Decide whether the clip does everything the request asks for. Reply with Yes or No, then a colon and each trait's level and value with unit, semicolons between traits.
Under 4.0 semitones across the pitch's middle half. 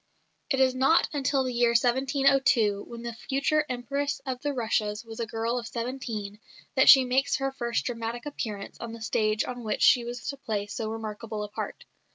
Yes: average, 3.1 semitones